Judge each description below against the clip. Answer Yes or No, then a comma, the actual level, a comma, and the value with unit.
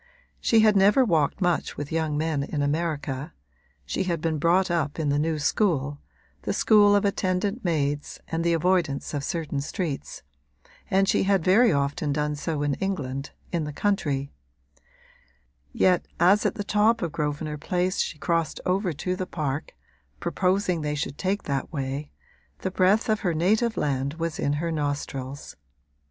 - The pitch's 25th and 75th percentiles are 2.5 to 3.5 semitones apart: No, average, 4.5 semitones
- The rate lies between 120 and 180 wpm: Yes, average, 165 wpm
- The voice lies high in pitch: No, medium, 165 Hz